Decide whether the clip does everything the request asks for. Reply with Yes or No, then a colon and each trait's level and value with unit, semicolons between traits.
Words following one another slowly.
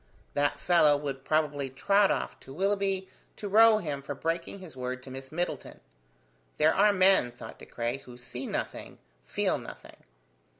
No: average, 165 wpm